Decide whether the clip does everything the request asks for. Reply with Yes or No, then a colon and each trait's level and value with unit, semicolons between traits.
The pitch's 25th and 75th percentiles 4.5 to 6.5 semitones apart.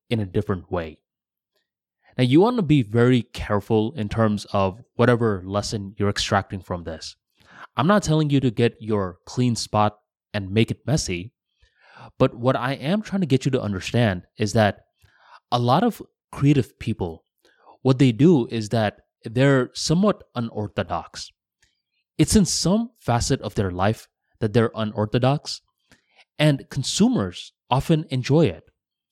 Yes: average, 4.8 semitones